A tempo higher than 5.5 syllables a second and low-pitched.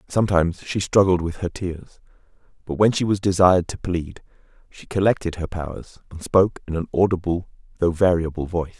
Yes: 5.9 syllables/s; very low, 90 Hz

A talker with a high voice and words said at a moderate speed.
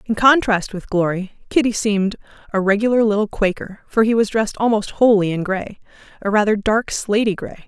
Yes: high, 210 Hz; average, 180 wpm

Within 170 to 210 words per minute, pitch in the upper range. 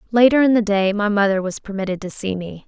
No: fast, 245 wpm; high, 205 Hz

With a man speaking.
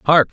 Yes: male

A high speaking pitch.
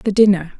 Yes: high, 195 Hz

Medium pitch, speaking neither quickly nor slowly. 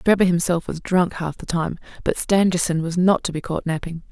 No: medium, 170 Hz; fast, 220 wpm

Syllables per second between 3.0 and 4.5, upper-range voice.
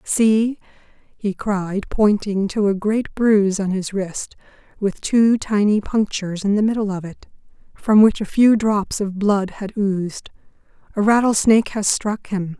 Yes: 4.2 syllables/s; high, 205 Hz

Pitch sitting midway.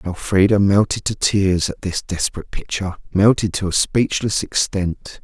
No: very low, 95 Hz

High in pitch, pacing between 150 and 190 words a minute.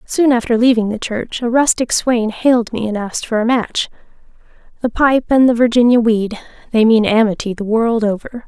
Yes: high, 230 Hz; average, 185 wpm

